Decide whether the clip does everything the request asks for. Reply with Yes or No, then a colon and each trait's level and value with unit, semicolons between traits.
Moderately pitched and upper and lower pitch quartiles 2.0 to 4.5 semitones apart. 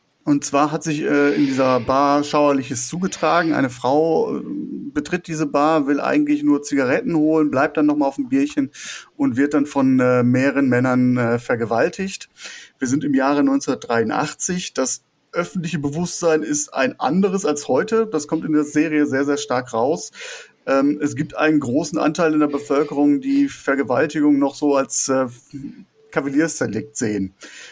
Yes: medium, 145 Hz; average, 2.9 semitones